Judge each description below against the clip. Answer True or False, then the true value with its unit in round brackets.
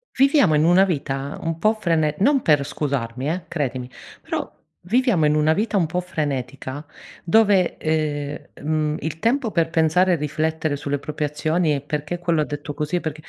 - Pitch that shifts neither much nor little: True (3.2 semitones)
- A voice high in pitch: False (155 Hz)